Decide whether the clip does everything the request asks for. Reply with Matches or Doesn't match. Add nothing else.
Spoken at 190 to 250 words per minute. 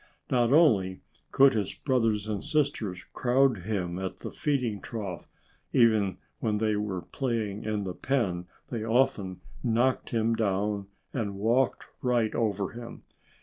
Doesn't match